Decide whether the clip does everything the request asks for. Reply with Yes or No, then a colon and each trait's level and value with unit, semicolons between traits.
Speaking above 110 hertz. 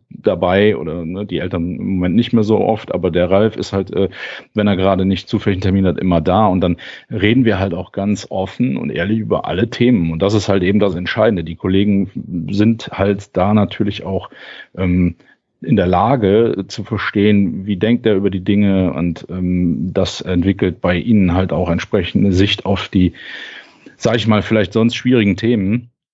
No: low, 100 Hz